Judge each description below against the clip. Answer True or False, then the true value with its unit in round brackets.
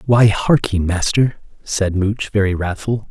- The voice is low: True (100 Hz)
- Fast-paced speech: False (135 wpm)